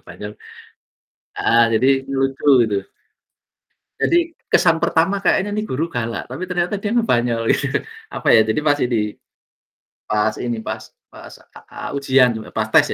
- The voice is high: No, low, 130 Hz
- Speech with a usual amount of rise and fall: No, wide, 8.1 semitones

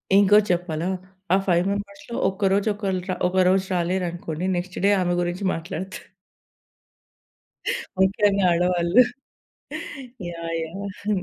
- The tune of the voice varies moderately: No, narrow, 2.3 semitones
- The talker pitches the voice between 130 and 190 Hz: Yes, medium, 185 Hz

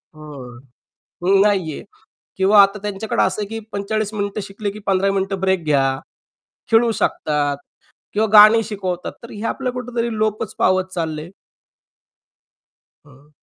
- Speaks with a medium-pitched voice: No, high, 195 Hz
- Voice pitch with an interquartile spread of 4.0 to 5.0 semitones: Yes, average, 4.7 semitones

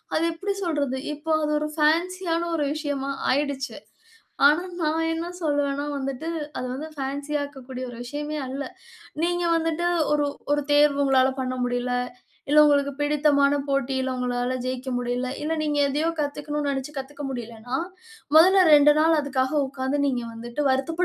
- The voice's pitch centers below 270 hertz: No, very high, 285 Hz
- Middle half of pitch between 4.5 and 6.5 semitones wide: No, narrow, 2.5 semitones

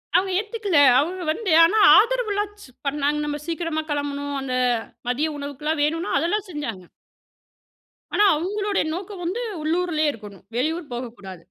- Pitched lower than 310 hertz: No, very high, 315 Hz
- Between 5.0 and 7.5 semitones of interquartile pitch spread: Yes, average, 5.3 semitones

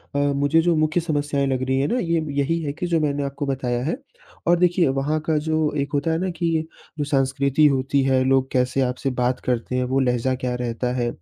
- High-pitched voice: No, medium, 140 Hz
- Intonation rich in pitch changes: No, average, 3.3 semitones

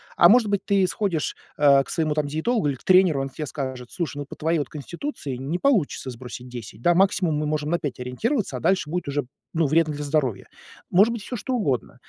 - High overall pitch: No, medium, 155 Hz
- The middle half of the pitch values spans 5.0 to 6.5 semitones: Yes, average, 5.3 semitones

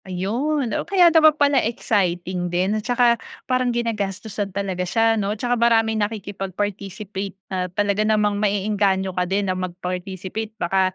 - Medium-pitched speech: No, high, 205 Hz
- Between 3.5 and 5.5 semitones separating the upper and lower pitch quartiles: No, average, 3.1 semitones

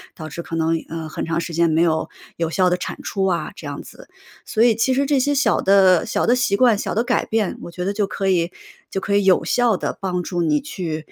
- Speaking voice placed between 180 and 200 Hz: Yes, high, 190 Hz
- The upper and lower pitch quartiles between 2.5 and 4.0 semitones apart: No, average, 4.7 semitones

